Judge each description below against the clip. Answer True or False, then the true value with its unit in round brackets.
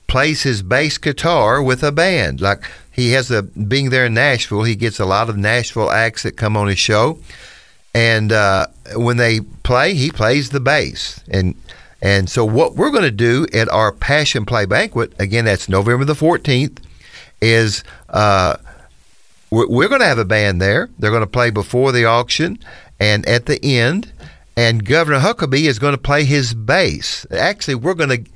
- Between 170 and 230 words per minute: True (185 wpm)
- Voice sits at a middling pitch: False (120 Hz)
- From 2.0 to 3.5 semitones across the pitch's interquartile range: False (4.3 semitones)